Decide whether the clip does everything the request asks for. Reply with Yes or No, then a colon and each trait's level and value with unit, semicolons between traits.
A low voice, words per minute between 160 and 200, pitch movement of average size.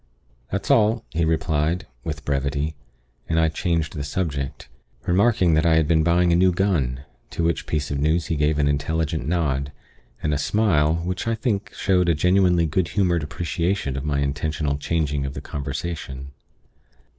Yes: very low, 80 Hz; average, 170 wpm; average, 3.3 semitones